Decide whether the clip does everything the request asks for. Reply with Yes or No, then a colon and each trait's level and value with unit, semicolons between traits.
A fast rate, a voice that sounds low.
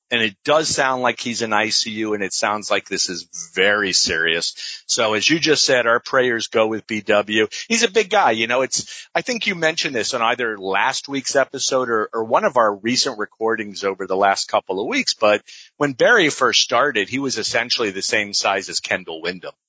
Yes: fast, 215 wpm; low, 115 Hz